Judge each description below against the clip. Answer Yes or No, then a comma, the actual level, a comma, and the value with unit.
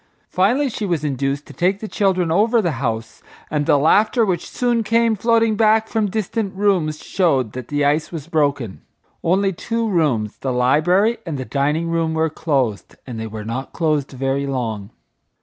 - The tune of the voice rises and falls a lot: Yes, wide, 6.9 semitones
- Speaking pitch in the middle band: Yes, medium, 160 Hz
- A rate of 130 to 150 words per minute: No, average, 180 wpm